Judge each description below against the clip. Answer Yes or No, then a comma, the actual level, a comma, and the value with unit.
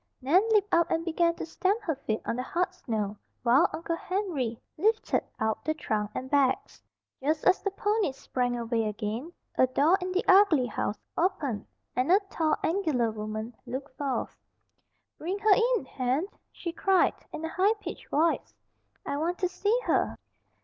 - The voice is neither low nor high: No, very high, 315 Hz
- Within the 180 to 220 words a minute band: No, average, 170 wpm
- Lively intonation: Yes, wide, 6.7 semitones